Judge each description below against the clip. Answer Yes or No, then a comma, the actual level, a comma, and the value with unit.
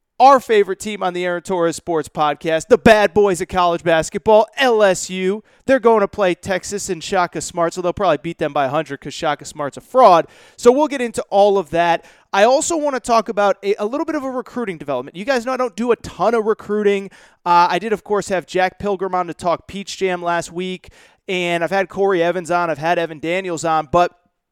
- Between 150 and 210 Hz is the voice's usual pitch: Yes, medium, 185 Hz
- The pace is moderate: No, fast, 230 wpm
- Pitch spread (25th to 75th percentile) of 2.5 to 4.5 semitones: Yes, average, 3.6 semitones